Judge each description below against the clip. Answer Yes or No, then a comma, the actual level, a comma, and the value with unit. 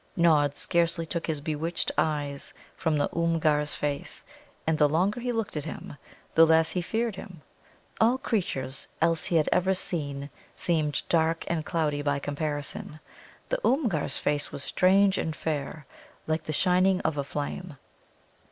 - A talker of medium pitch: Yes, medium, 160 Hz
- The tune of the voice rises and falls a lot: No, average, 3.4 semitones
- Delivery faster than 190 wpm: No, average, 155 wpm